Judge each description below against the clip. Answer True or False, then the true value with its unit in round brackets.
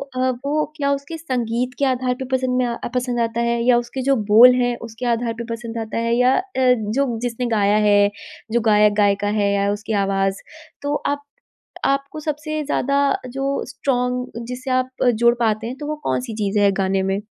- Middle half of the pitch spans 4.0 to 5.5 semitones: False (3.5 semitones)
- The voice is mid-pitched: False (245 Hz)